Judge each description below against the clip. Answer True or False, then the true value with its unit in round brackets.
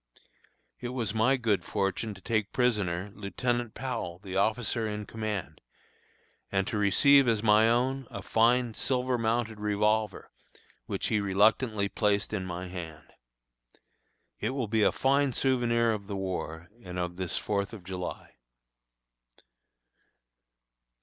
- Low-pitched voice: True (105 Hz)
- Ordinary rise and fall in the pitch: True (3.4 semitones)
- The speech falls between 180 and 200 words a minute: False (135 wpm)